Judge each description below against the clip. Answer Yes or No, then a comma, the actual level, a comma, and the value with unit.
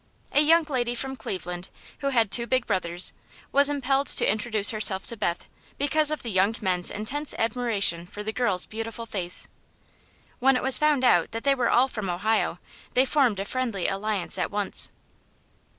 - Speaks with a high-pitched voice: Yes, high, 225 Hz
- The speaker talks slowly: No, average, 175 wpm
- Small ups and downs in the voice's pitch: No, average, 5.1 semitones